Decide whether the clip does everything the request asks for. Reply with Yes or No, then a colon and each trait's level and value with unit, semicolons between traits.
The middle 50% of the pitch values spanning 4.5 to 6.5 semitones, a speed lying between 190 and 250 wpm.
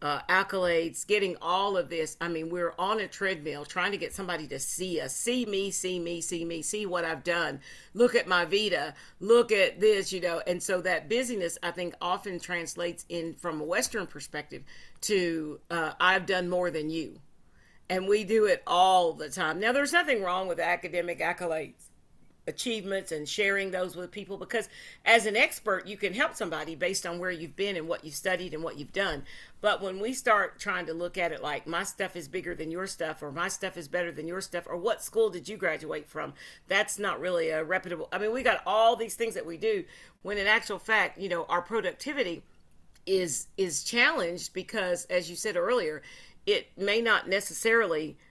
No: average, 3.4 semitones; fast, 205 wpm